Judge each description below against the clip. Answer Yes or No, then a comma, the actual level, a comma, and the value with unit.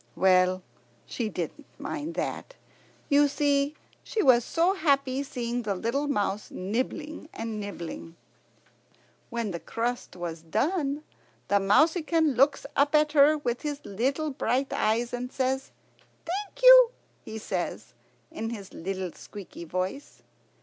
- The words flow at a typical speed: No, slow, 130 wpm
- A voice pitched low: No, very high, 255 Hz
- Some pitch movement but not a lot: No, wide, 6.4 semitones